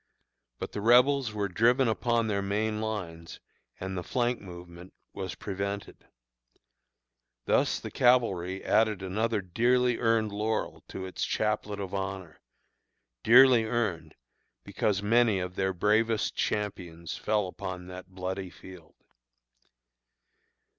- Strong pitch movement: No, average, 3.4 semitones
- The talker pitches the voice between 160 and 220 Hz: No, low, 100 Hz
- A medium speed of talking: No, slow, 120 wpm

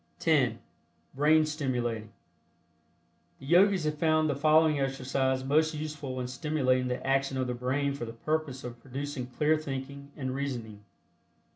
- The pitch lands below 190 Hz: Yes, low, 135 Hz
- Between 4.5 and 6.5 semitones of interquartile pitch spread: No, average, 3.0 semitones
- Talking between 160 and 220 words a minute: No, average, 145 wpm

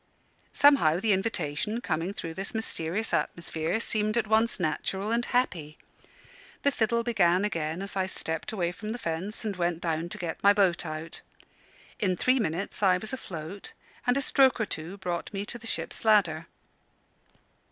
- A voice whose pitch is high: Yes, high, 195 Hz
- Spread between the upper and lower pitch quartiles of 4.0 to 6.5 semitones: Yes, average, 4.7 semitones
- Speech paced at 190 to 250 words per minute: No, average, 170 wpm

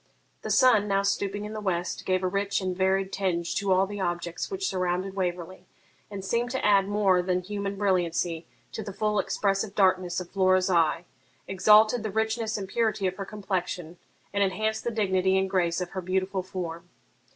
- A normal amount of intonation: No, narrow, 2.0 semitones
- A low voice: No, high, 190 Hz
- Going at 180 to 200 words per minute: Yes, average, 185 wpm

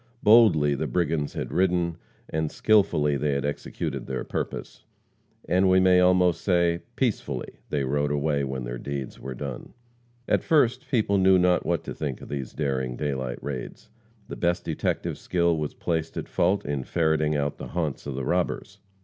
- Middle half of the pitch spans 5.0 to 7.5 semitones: No, average, 4.3 semitones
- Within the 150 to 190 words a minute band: Yes, average, 175 wpm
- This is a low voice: Yes, very low, 80 Hz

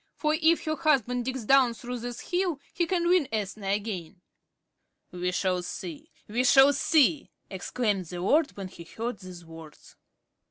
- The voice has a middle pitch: No, high, 235 Hz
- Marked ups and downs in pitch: Yes, wide, 7.5 semitones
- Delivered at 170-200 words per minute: No, average, 160 wpm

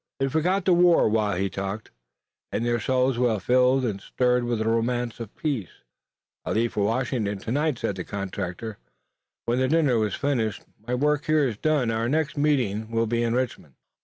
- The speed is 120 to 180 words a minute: No, average, 190 wpm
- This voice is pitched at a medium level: No, low, 120 Hz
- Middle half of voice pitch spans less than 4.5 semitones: Yes, average, 3.8 semitones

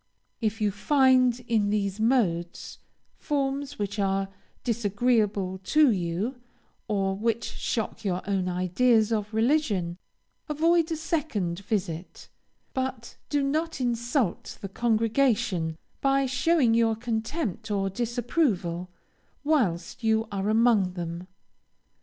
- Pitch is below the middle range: No, high, 220 Hz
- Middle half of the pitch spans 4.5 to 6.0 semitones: Yes, average, 5.0 semitones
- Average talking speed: No, slow, 110 wpm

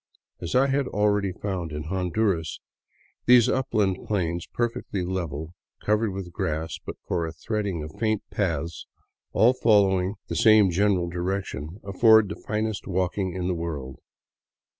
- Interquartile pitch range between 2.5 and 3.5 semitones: No, average, 3.9 semitones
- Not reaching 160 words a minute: Yes, average, 145 wpm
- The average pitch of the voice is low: Yes, very low, 95 Hz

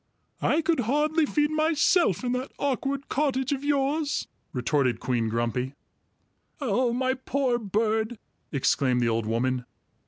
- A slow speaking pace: Yes, slow, 130 wpm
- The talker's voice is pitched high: Yes, very high, 250 Hz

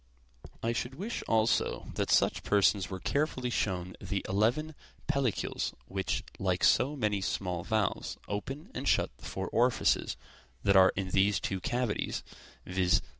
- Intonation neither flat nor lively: Yes, average, 4.6 semitones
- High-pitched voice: No, low, 105 Hz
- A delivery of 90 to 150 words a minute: Yes, average, 145 wpm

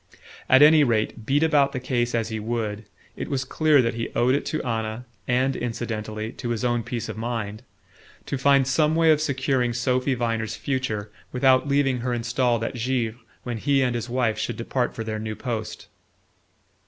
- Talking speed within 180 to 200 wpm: Yes, average, 190 wpm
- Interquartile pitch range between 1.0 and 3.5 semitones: Yes, average, 2.8 semitones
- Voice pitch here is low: Yes, low, 120 Hz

